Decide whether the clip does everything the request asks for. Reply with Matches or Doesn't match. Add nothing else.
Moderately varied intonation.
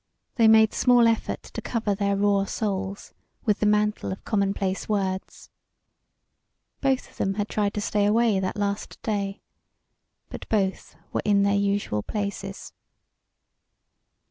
Doesn't match